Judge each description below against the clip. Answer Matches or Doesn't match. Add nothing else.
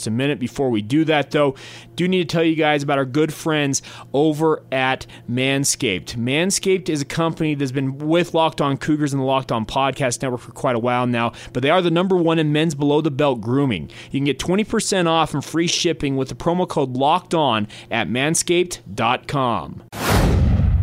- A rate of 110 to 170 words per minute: Doesn't match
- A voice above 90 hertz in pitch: Matches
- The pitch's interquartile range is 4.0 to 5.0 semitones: Matches